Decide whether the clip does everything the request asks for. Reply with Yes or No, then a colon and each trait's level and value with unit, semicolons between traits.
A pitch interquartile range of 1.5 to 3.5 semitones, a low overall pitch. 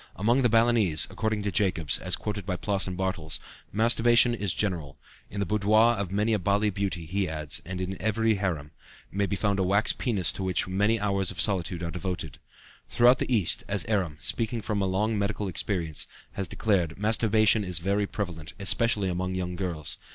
Yes: average, 2.9 semitones; low, 100 Hz